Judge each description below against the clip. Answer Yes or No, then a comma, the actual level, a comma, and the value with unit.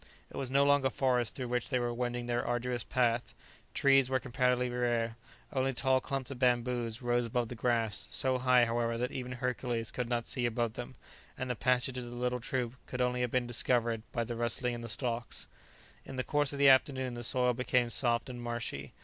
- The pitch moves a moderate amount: No, narrow, 1.3 semitones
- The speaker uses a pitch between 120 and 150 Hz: Yes, low, 125 Hz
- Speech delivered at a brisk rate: Yes, fast, 210 wpm